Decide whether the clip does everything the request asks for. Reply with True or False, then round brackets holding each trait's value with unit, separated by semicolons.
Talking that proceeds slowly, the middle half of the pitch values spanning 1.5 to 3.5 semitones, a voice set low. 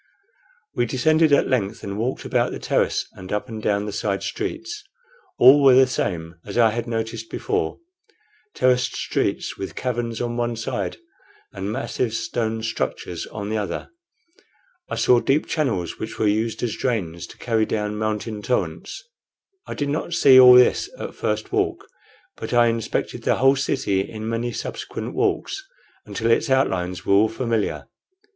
False (165 wpm; 3.2 semitones; 115 Hz)